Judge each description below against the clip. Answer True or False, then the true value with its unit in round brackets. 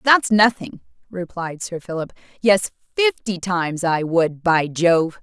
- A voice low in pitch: False (185 Hz)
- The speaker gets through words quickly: False (140 wpm)